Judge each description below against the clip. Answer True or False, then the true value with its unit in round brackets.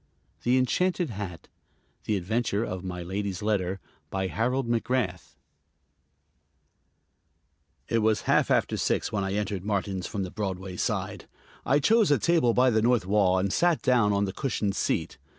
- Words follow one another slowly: False (155 wpm)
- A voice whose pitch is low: True (105 Hz)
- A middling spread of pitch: True (4.3 semitones)